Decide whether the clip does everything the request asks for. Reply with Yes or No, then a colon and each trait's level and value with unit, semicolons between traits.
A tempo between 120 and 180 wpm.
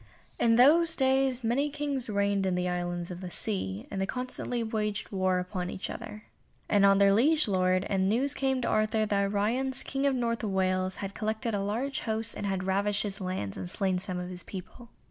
No: fast, 205 wpm